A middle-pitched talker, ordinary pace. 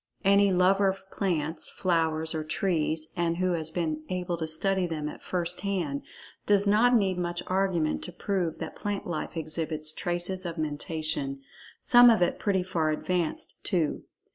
Yes: medium, 175 Hz; average, 165 wpm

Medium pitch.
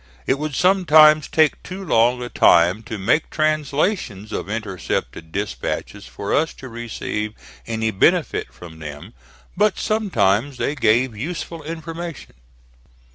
No: low, 125 Hz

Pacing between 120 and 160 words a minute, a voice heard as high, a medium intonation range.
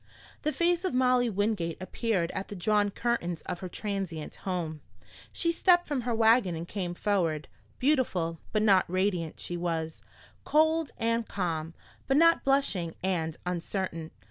No: average, 150 wpm; high, 195 Hz; wide, 6.3 semitones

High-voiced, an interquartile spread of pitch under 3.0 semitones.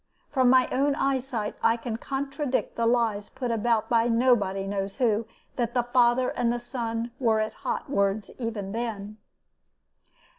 Yes: high, 235 Hz; narrow, 2.6 semitones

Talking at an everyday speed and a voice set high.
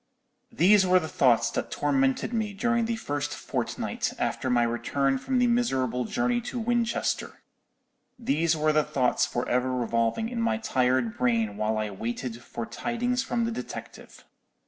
No: average, 160 wpm; medium, 145 Hz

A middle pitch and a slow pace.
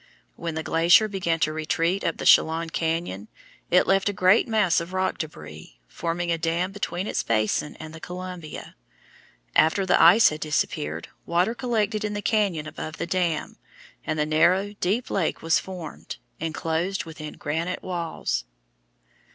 No: medium, 170 Hz; average, 160 wpm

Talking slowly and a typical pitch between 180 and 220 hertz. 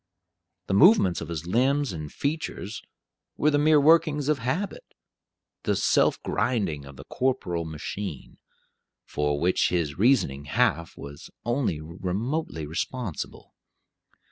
No: slow, 120 wpm; very low, 95 Hz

